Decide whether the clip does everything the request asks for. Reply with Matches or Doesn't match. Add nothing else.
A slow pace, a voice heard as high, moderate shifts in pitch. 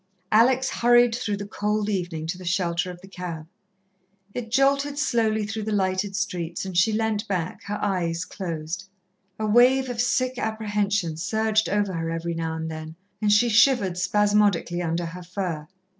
Doesn't match